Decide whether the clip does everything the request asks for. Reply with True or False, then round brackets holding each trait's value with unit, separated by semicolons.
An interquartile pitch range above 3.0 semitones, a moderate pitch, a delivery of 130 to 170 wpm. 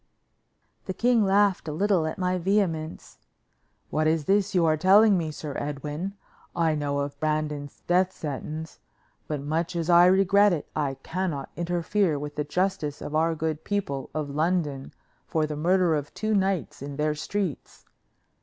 True (3.9 semitones; 160 Hz; 165 wpm)